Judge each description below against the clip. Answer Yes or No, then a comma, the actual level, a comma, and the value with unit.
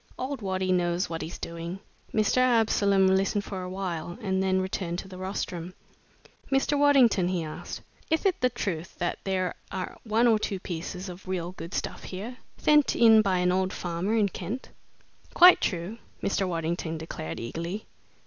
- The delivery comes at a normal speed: Yes, average, 170 wpm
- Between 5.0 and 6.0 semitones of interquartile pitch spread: No, average, 3.7 semitones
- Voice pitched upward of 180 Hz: Yes, high, 190 Hz